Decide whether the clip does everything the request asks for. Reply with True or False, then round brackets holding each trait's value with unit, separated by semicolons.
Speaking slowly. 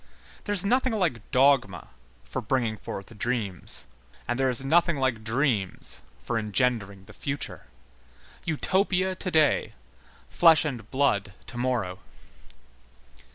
True (120 wpm)